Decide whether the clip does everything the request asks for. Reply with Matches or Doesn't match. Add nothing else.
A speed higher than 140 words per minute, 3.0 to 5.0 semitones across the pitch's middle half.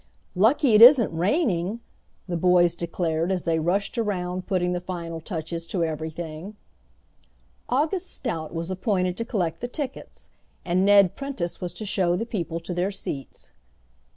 Matches